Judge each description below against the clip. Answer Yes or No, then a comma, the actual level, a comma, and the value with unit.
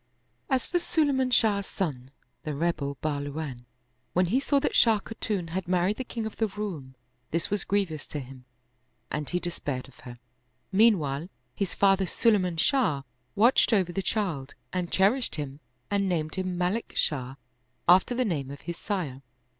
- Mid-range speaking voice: Yes, medium, 180 Hz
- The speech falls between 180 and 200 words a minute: No, average, 170 wpm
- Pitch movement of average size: No, wide, 6.0 semitones